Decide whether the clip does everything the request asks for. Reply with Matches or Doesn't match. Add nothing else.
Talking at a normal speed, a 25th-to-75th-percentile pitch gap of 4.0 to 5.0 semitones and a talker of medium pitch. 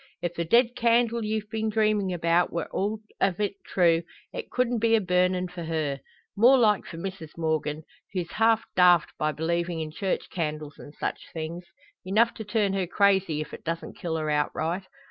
Matches